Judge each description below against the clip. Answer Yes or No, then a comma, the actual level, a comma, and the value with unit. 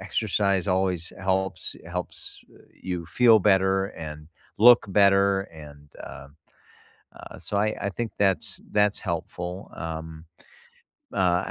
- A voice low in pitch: Yes, very low, 95 Hz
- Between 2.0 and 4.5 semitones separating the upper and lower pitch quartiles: Yes, average, 2.7 semitones